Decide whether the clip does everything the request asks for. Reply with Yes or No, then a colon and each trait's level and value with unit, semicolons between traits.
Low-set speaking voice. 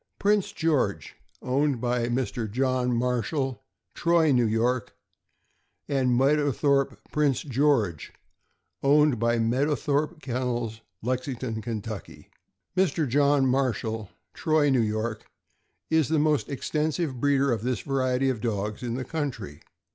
Yes: low, 130 Hz